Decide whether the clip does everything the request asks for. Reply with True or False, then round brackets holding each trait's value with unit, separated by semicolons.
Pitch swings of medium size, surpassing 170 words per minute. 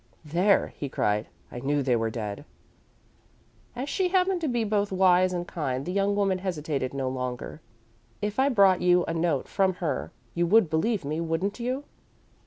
False (6.0 semitones; 180 wpm)